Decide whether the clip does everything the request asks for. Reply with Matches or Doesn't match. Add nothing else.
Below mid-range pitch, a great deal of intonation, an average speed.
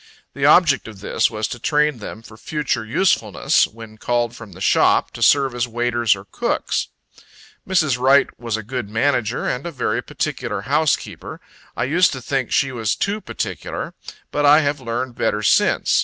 Doesn't match